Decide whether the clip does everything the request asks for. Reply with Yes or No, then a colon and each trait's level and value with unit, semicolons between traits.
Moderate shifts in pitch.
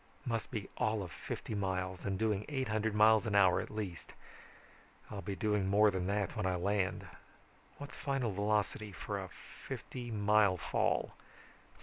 No: narrow, 2.1 semitones